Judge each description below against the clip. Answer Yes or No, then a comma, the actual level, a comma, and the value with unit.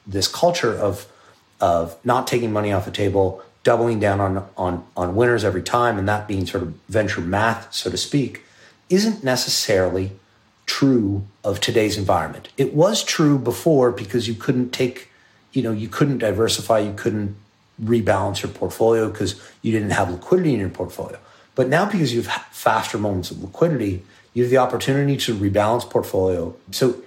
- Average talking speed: Yes, average, 170 wpm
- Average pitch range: Yes, average, 3.9 semitones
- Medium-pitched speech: No, low, 110 Hz